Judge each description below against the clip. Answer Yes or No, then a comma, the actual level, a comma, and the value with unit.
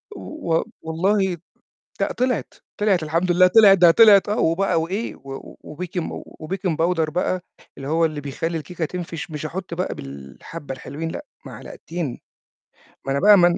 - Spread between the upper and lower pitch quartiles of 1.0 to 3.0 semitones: No, average, 3.4 semitones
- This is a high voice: No, medium, 170 Hz